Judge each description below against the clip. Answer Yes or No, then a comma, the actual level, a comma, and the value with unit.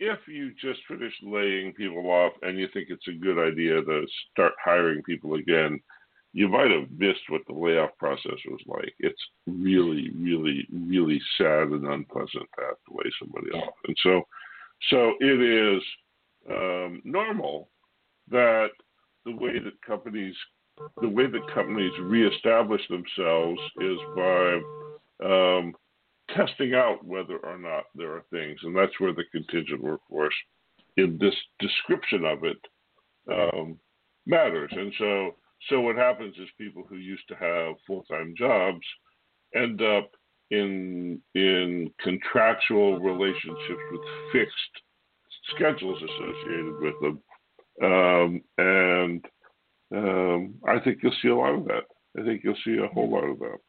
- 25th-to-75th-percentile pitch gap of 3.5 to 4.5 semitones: No, average, 3.0 semitones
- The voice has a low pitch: Yes, very low, 90 Hz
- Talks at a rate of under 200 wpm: Yes, average, 145 wpm